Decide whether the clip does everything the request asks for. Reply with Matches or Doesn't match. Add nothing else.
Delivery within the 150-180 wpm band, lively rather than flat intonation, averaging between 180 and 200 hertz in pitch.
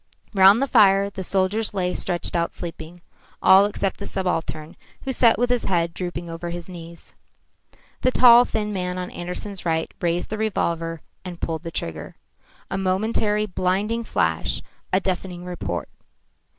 Doesn't match